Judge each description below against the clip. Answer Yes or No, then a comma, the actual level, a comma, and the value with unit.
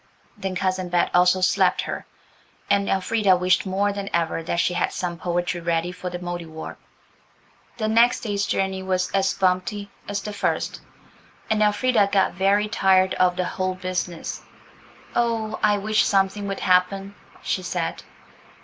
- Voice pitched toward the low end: No, high, 190 Hz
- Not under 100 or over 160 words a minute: Yes, average, 155 wpm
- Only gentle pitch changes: Yes, narrow, 2.1 semitones